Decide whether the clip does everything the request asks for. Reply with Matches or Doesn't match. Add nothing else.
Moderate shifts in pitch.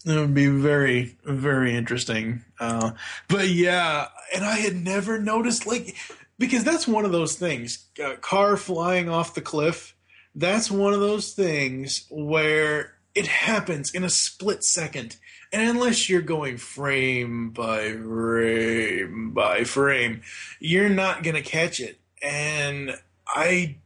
Doesn't match